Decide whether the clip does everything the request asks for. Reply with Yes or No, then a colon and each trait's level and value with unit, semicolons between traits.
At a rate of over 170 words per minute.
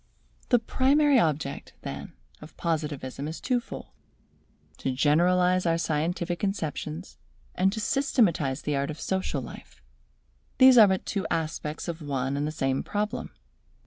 No: average, 145 wpm